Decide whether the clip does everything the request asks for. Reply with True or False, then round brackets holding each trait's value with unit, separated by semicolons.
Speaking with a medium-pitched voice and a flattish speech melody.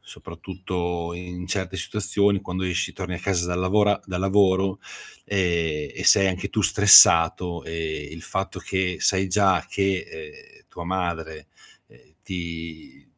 False (90 Hz; 2.2 semitones)